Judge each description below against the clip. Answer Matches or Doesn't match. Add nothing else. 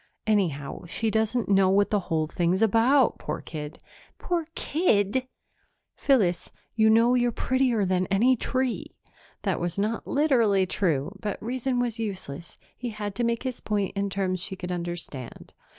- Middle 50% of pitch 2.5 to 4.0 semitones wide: Doesn't match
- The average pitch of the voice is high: Matches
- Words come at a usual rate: Matches